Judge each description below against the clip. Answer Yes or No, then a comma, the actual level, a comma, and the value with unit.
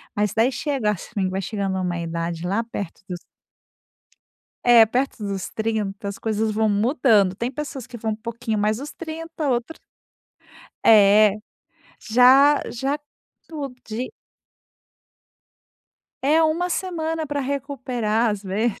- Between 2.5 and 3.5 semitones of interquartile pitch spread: No, average, 5.1 semitones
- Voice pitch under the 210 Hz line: No, high, 225 Hz